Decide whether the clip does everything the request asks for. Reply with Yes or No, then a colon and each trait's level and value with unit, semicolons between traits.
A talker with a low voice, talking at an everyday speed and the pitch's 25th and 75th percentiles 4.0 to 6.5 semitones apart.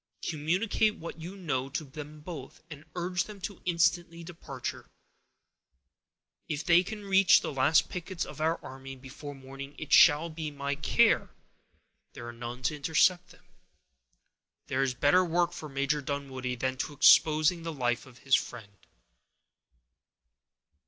No: medium, 150 Hz; average, 150 wpm; average, 4.3 semitones